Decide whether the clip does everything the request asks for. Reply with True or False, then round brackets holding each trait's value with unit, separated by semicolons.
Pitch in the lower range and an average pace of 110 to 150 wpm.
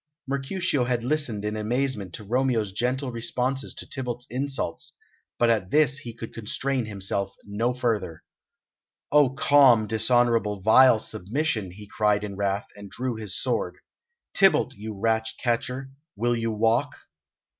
True (115 Hz; 140 wpm)